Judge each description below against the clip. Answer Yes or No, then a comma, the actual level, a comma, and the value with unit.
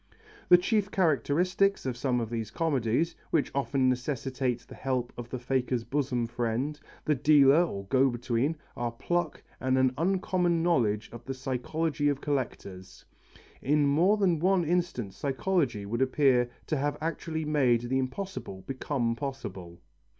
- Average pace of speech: Yes, average, 150 wpm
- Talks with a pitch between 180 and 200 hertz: No, low, 135 Hz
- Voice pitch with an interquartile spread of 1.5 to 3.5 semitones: No, average, 4.7 semitones